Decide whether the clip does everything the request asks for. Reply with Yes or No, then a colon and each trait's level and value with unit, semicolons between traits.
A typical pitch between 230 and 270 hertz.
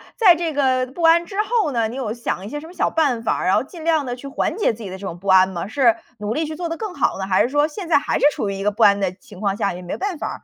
Yes: very high, 255 Hz